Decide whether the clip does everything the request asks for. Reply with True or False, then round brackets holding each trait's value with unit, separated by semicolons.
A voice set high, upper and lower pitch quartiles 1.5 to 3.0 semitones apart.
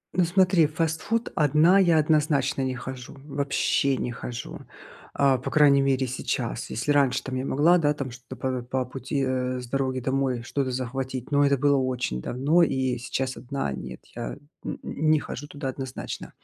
False (135 Hz; 2.4 semitones)